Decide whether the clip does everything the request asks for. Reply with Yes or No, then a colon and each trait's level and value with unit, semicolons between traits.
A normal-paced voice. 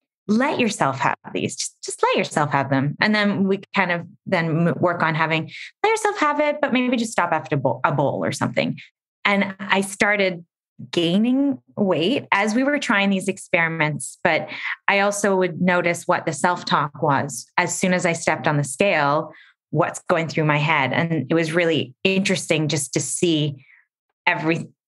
Yes: average, 185 wpm